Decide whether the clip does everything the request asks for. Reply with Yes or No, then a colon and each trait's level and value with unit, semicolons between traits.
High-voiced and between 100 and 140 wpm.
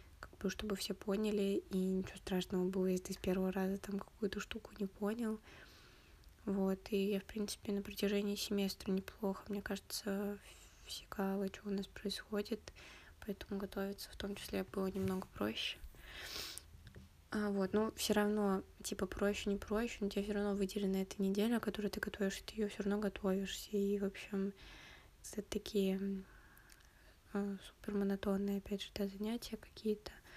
No: high, 200 Hz; average, 155 wpm